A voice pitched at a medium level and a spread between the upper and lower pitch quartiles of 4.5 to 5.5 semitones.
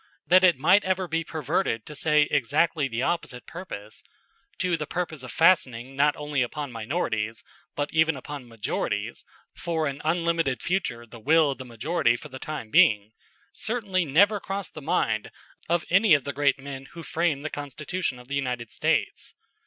Yes: medium, 150 Hz; average, 5.0 semitones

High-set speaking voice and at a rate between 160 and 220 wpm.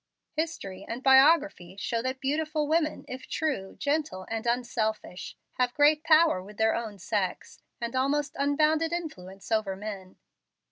No: very high, 255 Hz; average, 140 wpm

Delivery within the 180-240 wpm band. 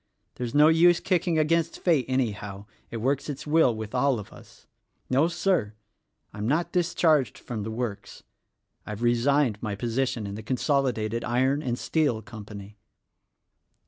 No: average, 145 wpm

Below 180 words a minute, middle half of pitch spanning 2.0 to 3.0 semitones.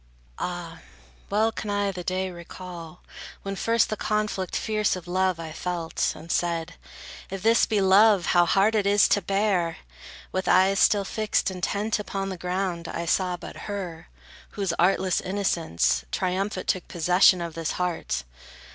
Yes: average, 155 wpm; narrow, 2.6 semitones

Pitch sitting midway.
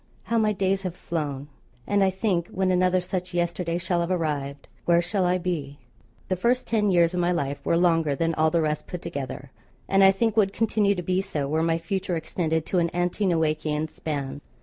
Yes: medium, 175 Hz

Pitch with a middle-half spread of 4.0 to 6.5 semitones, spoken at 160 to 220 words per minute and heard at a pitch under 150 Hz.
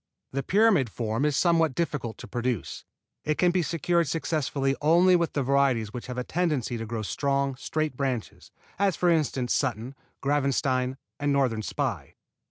Yes: average, 4.3 semitones; average, 165 wpm; medium, 140 Hz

